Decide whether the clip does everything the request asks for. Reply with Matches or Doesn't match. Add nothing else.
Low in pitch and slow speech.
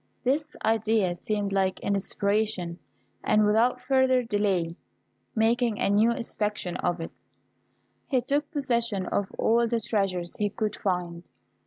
Doesn't match